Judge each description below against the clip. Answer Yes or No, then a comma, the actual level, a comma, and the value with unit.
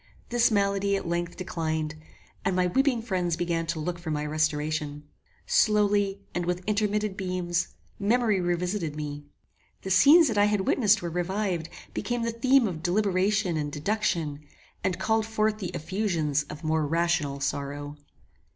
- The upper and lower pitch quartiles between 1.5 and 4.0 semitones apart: No, average, 4.7 semitones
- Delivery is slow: No, average, 150 wpm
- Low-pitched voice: No, medium, 180 Hz